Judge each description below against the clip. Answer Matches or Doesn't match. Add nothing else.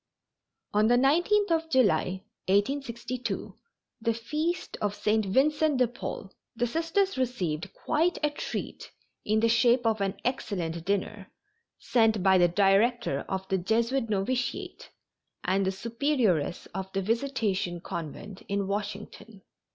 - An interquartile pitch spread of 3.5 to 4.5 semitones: Doesn't match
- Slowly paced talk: Matches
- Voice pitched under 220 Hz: Doesn't match